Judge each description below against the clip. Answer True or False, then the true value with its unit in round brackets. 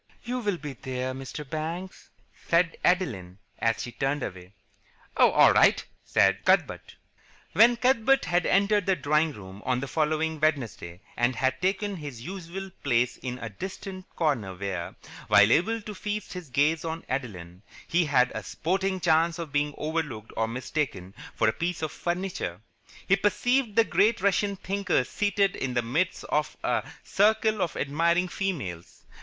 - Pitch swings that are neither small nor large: False (7.2 semitones)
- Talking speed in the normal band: True (160 wpm)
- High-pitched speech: False (160 Hz)